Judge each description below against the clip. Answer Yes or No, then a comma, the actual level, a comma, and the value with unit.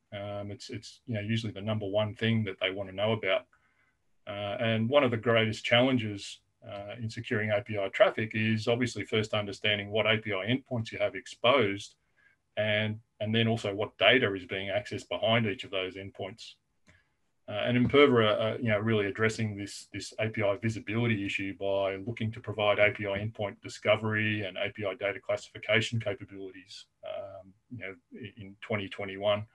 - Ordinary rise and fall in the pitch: No, narrow, 2.2 semitones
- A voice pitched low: Yes, low, 105 Hz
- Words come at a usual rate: Yes, average, 165 wpm